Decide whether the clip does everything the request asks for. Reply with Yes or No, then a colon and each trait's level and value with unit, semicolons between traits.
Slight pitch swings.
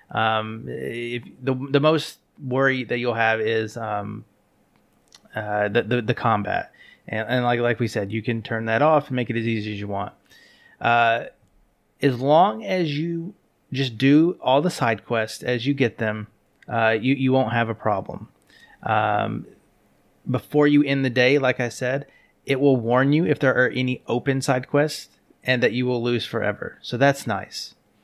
No: average, 3.5 semitones